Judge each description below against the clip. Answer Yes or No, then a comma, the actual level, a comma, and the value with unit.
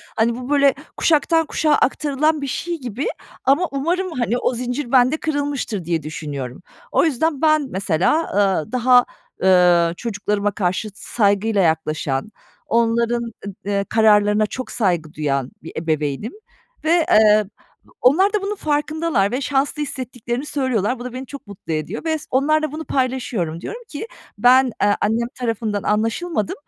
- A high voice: Yes, high, 240 Hz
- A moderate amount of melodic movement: No, wide, 6.1 semitones